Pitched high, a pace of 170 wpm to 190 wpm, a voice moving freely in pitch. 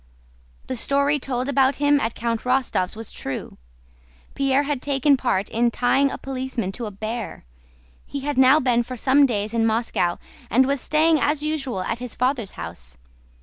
No: very high, 255 Hz; average, 175 wpm; average, 3.5 semitones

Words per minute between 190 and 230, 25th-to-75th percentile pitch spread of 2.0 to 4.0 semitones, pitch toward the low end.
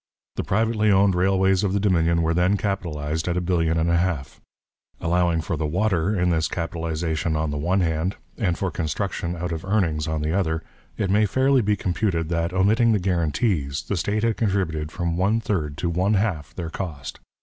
Yes: average, 195 wpm; average, 3.3 semitones; very low, 90 Hz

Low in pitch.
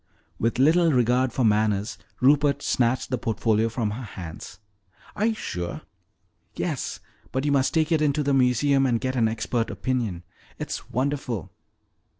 Yes: low, 125 Hz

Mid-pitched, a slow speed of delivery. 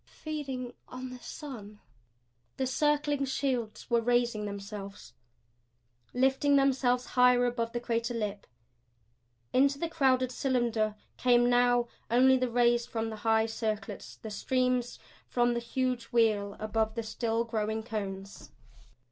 No: high, 240 Hz; slow, 130 wpm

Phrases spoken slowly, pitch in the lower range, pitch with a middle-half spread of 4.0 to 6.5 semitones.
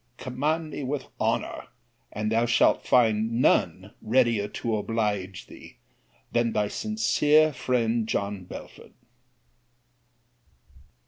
No: slow, 105 wpm; low, 115 Hz; average, 3.0 semitones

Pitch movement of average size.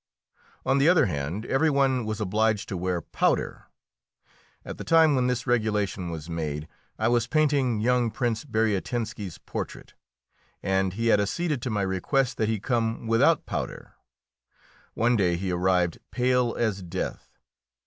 Yes: average, 4.8 semitones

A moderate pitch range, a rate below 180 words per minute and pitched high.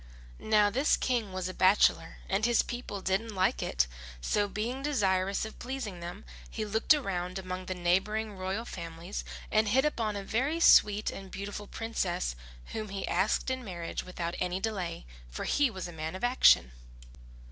Yes: average, 3.4 semitones; average, 170 wpm; high, 200 Hz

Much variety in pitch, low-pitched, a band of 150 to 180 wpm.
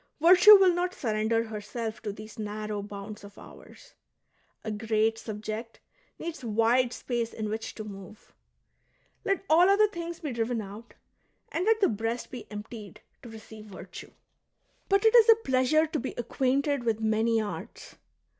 No: wide, 6.4 semitones; high, 230 Hz; average, 160 wpm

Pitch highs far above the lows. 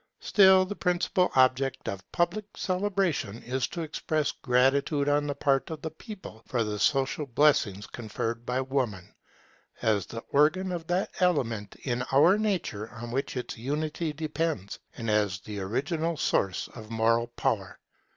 Yes: wide, 6.0 semitones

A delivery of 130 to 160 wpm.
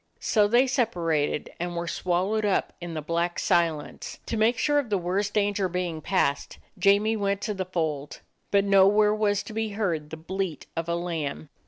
No: average, 185 wpm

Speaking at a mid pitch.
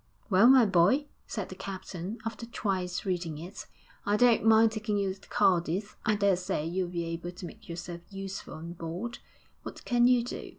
No: high, 195 Hz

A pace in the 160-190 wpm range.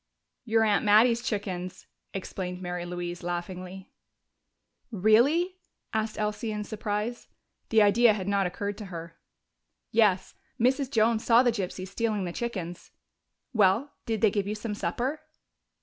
No: slow, 135 wpm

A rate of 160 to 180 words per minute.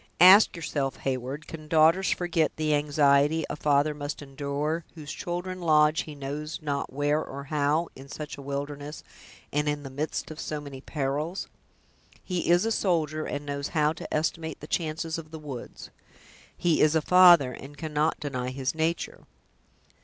Yes: average, 170 wpm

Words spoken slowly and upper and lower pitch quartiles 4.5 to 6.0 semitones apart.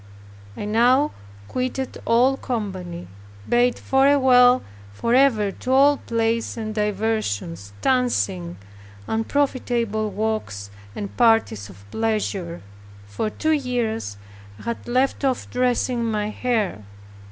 No: slow, 105 wpm; average, 3.7 semitones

